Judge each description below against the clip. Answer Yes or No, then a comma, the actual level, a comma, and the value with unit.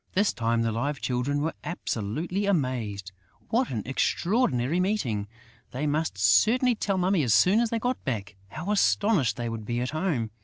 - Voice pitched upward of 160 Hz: No, medium, 145 Hz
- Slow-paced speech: No, average, 175 wpm